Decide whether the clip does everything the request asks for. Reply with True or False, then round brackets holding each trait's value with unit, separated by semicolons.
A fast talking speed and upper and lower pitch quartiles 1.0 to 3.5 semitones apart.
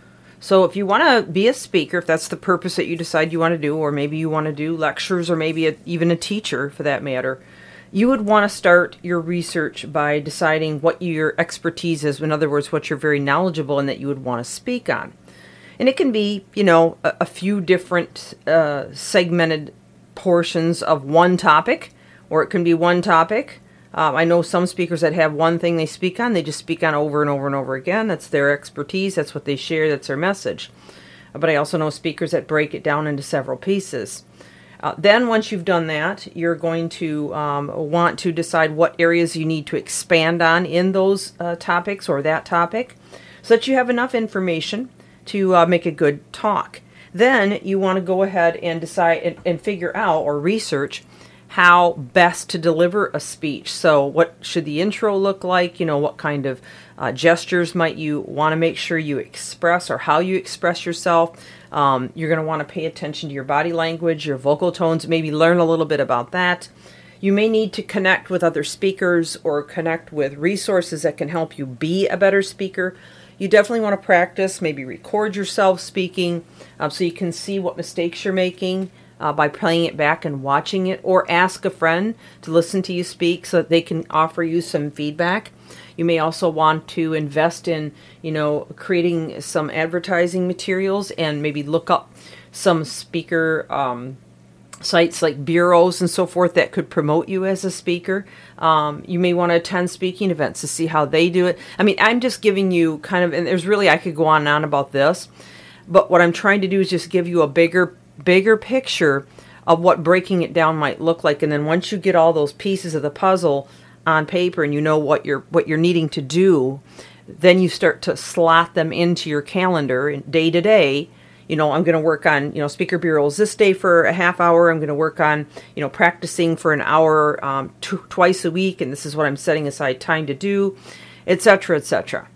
True (210 wpm; 3.0 semitones)